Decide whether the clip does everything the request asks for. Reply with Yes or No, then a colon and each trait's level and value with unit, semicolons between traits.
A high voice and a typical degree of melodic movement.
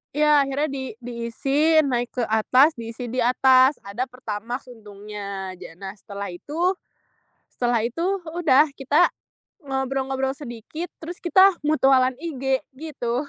Yes: very high, 260 Hz; average, 4.1 semitones